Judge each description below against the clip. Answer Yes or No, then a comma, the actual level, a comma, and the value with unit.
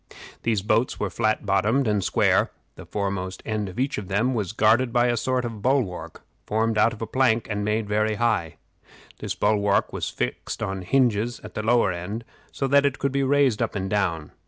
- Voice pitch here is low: Yes, low, 110 Hz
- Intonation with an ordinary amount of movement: Yes, average, 3.1 semitones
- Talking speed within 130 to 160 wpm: No, average, 195 wpm